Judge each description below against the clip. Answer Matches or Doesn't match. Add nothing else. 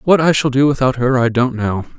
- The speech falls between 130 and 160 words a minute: Doesn't match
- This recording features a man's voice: Matches